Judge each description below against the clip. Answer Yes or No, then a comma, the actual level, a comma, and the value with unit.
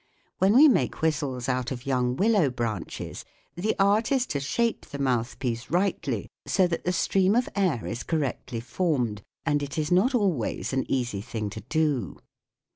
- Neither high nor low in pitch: Yes, medium, 145 Hz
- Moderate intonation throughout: No, wide, 7.3 semitones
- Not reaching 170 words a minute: No, average, 180 wpm